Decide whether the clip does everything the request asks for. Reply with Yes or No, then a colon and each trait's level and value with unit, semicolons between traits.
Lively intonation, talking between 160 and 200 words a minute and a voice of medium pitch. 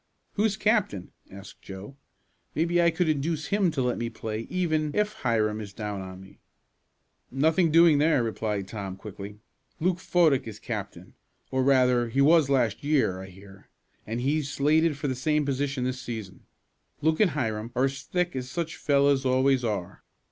No: wide, 6.3 semitones; average, 170 wpm; low, 130 Hz